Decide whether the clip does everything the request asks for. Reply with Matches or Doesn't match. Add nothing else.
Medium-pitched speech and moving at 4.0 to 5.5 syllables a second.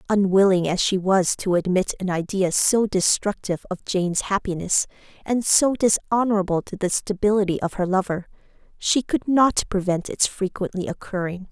Doesn't match